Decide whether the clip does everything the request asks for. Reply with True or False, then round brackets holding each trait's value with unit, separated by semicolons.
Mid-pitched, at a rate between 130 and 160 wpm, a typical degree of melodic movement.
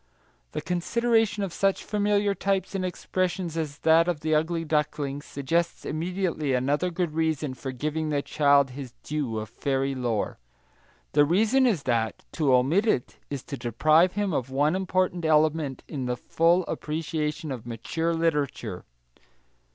True (155 Hz; 150 wpm; 4.3 semitones)